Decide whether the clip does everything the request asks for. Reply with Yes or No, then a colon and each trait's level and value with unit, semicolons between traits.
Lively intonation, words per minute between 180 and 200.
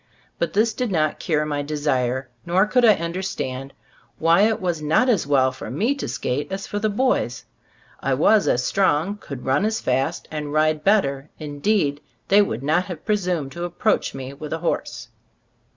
Yes: wide, 6.2 semitones; average, 185 wpm